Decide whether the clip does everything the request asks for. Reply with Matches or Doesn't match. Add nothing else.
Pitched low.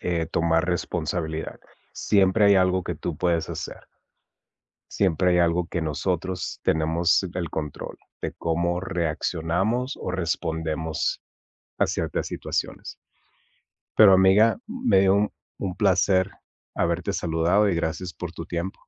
Matches